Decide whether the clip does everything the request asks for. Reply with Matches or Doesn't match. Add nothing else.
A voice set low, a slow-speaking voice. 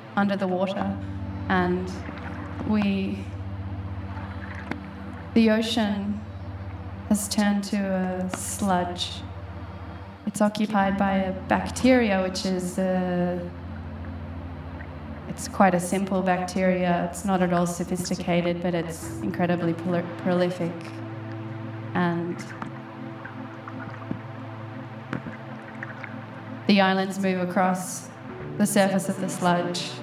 Matches